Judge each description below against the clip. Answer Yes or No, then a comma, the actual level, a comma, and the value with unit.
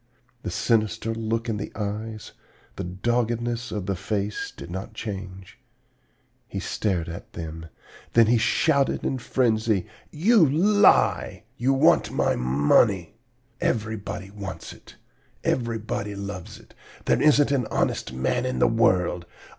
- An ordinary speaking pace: No, slow, 130 wpm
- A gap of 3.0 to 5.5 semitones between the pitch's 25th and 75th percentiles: Yes, average, 3.8 semitones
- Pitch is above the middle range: No, low, 110 Hz